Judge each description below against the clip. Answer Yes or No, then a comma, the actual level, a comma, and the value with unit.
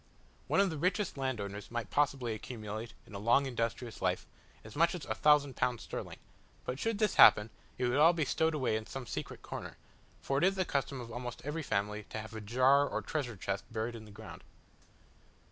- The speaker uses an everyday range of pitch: Yes, average, 5.0 semitones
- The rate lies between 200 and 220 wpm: Yes, fast, 205 wpm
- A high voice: No, low, 125 Hz